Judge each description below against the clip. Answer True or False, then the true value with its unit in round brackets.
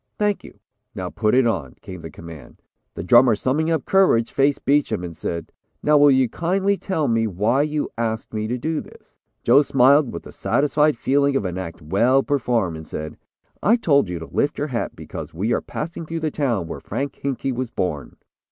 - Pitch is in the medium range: False (125 Hz)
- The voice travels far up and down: True (7.4 semitones)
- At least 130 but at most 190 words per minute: False (205 wpm)